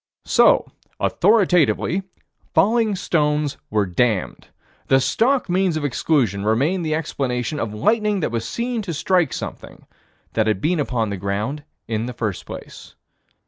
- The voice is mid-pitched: Yes, medium, 145 Hz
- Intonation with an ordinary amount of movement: No, wide, 8.5 semitones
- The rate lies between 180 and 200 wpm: No, average, 140 wpm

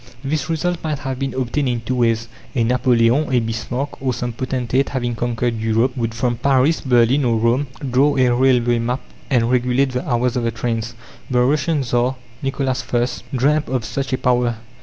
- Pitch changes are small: Yes, narrow, 2.2 semitones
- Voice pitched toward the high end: No, low, 125 Hz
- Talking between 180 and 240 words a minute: Yes, average, 185 wpm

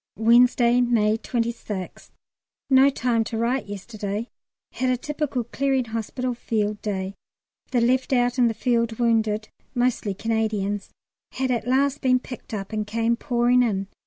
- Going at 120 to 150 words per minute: Yes, average, 145 wpm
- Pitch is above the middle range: Yes, high, 235 Hz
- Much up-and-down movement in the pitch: No, narrow, 2.6 semitones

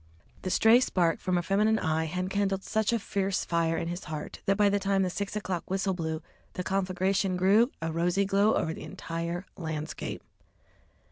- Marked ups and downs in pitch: No, average, 2.9 semitones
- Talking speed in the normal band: Yes, average, 190 wpm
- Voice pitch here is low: No, medium, 185 Hz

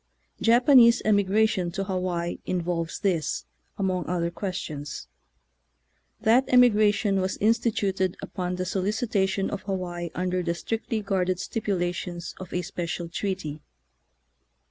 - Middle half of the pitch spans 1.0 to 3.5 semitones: Yes, average, 2.9 semitones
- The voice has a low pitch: No, medium, 185 Hz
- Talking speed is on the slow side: Yes, slow, 115 wpm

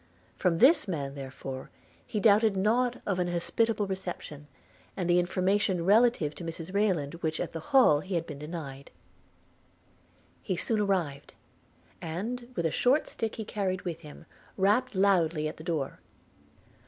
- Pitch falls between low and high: Yes, medium, 180 Hz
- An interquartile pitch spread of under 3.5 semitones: No, average, 4.6 semitones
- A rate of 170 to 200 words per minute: No, average, 155 wpm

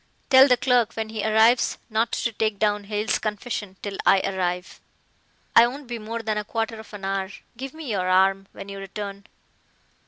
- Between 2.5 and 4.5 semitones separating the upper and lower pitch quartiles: Yes, average, 2.9 semitones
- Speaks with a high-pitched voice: Yes, high, 215 Hz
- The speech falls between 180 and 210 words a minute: Yes, average, 190 wpm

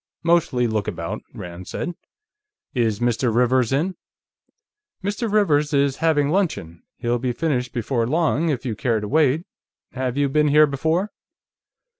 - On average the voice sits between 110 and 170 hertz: Yes, low, 135 Hz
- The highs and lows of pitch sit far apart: No, average, 4.8 semitones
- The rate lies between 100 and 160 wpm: Yes, average, 150 wpm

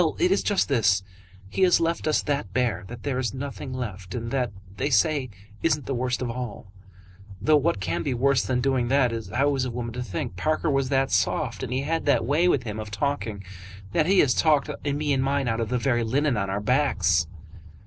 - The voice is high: No, low, 130 Hz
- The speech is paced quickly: Yes, fast, 225 wpm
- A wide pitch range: No, average, 3.9 semitones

